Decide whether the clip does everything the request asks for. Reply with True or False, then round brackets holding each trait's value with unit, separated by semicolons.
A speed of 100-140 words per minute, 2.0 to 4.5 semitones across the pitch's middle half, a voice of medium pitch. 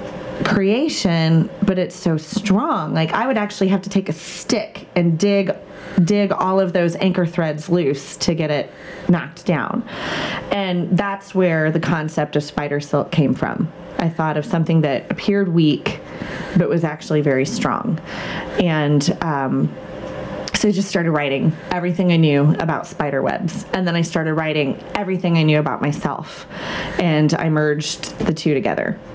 False (165 wpm; 3.8 semitones; 175 Hz)